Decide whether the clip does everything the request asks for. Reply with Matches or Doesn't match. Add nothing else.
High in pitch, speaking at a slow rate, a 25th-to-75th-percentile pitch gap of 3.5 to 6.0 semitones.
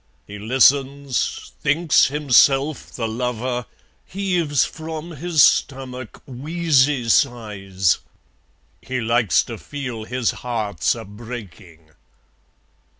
Doesn't match